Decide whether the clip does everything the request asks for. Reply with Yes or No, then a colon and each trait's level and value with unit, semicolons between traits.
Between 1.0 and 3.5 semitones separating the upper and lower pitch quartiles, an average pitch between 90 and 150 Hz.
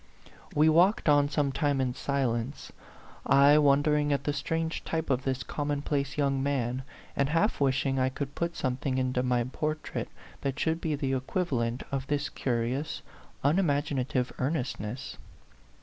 Yes: narrow, 2.4 semitones; medium, 140 Hz